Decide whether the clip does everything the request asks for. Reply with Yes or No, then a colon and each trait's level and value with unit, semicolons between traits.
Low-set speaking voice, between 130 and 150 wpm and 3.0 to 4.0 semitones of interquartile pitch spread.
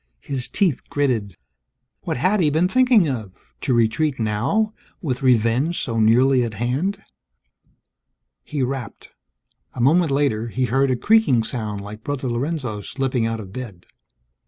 No: low, 130 Hz; average, 145 wpm; average, 4.7 semitones